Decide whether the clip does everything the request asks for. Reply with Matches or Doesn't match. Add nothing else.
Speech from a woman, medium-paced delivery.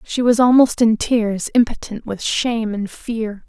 Matches